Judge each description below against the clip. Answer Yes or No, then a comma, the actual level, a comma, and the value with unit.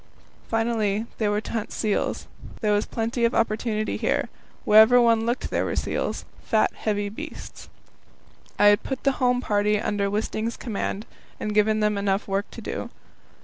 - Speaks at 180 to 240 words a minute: No, average, 170 wpm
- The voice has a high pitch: Yes, high, 215 Hz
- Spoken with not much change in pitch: Yes, narrow, 1.9 semitones